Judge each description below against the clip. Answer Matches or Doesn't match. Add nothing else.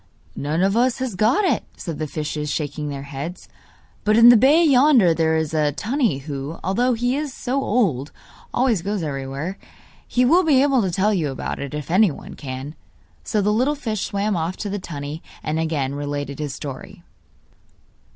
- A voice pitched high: Doesn't match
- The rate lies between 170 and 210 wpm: Matches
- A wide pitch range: Matches